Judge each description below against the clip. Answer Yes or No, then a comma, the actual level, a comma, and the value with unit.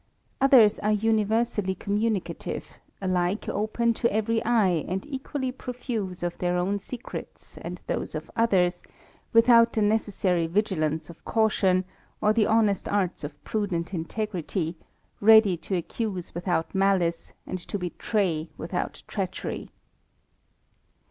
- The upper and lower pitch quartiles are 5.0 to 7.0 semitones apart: No, average, 3.9 semitones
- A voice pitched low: No, high, 200 Hz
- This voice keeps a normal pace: No, slow, 120 wpm